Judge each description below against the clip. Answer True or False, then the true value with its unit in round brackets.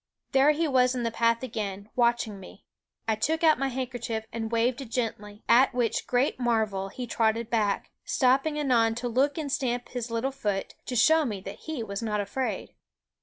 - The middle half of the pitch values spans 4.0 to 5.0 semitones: False (3.0 semitones)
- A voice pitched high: True (240 Hz)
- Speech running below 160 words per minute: False (190 wpm)